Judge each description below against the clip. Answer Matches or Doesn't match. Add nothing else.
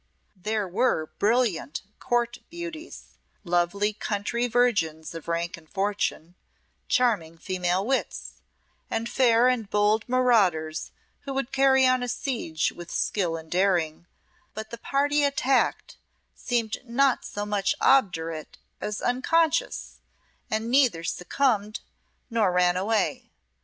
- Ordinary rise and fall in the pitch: Doesn't match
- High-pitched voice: Matches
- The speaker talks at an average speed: Doesn't match